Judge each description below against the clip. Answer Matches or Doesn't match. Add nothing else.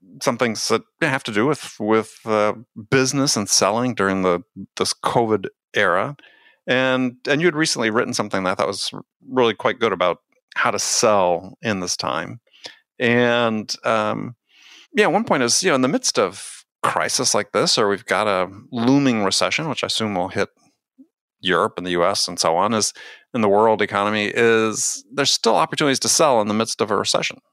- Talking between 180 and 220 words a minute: Matches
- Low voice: Matches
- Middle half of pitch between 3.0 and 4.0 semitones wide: Doesn't match